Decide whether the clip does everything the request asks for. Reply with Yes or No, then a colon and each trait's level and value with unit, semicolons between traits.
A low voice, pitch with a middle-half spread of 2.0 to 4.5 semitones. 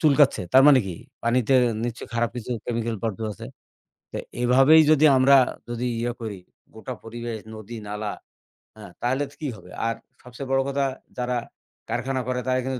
Yes: low, 125 Hz; average, 2.8 semitones